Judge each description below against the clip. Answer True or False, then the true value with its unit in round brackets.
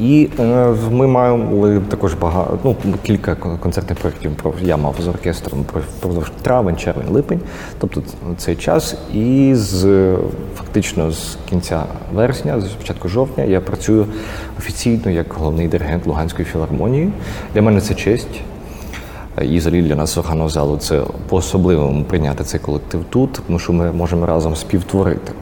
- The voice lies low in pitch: True (90 Hz)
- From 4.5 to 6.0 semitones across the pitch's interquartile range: False (4.0 semitones)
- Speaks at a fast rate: False (140 wpm)